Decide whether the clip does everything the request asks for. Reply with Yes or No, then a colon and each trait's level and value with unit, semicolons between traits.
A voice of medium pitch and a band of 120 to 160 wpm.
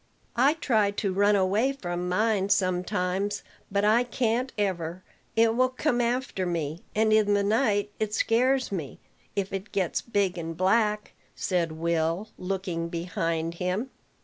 No: high, 200 Hz; average, 150 wpm